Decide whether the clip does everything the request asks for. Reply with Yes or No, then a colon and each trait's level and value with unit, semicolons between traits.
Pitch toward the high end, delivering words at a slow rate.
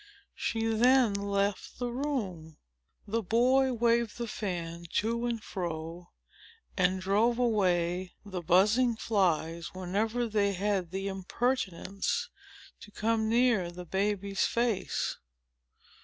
Yes: high, 205 Hz; slow, 110 wpm